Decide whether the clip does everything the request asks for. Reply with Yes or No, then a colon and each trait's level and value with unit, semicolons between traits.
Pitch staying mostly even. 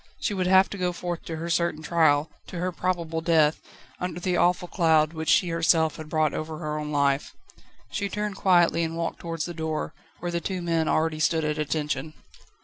Yes: narrow, 2.1 semitones